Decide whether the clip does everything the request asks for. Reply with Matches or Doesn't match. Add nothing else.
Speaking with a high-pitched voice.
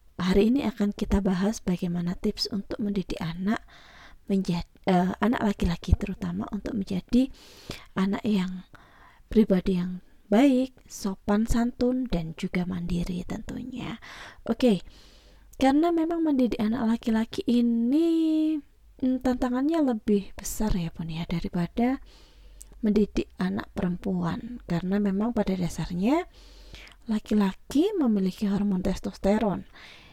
Matches